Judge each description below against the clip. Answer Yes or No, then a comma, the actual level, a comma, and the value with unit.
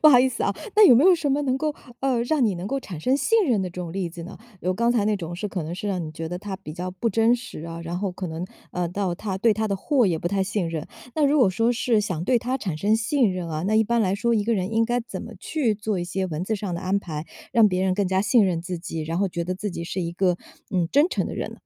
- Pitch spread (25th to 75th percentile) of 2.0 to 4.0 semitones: No, average, 4.8 semitones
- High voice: Yes, high, 200 Hz